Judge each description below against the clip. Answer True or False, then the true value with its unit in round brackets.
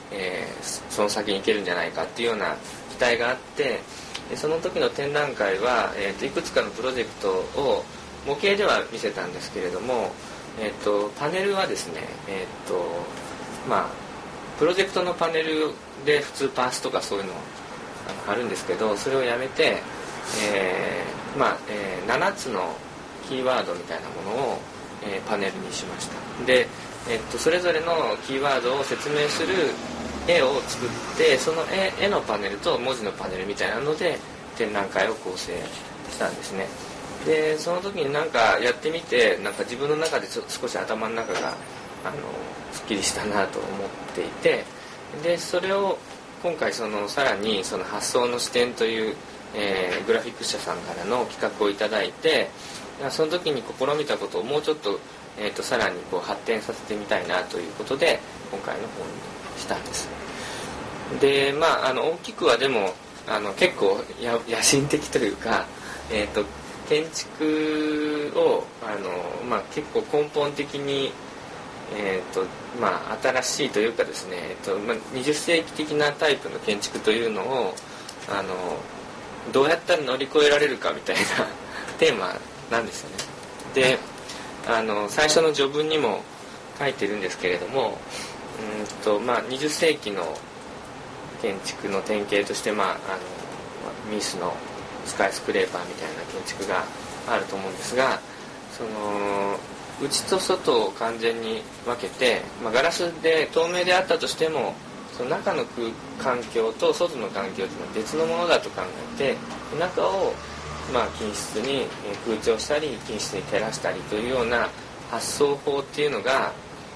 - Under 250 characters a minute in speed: False (305 characters per minute)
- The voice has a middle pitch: True (155 Hz)